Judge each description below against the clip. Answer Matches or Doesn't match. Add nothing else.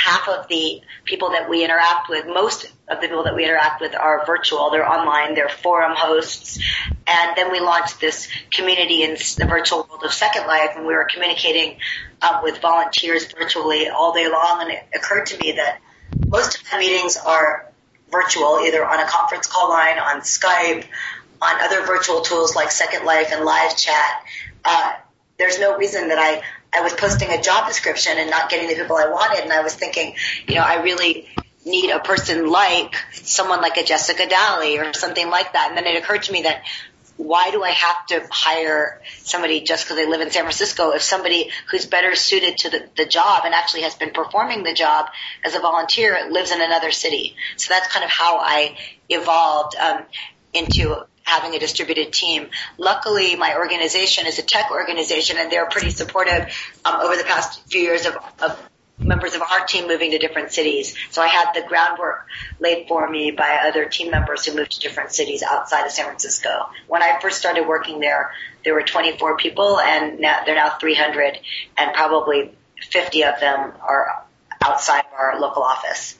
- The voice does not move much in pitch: Matches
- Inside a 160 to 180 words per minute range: Doesn't match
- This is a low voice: Doesn't match